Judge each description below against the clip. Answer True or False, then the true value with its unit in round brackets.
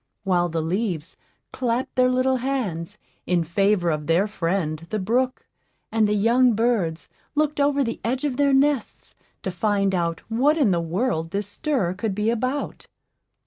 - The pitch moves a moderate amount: False (6.6 semitones)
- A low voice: False (210 Hz)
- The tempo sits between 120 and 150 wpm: False (165 wpm)